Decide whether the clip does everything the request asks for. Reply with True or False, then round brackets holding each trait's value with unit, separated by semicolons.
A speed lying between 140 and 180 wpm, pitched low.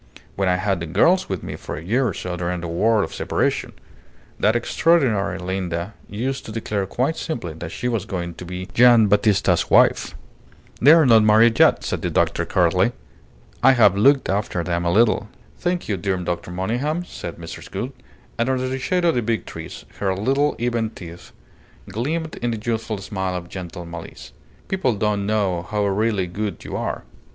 False (190 wpm; 105 Hz)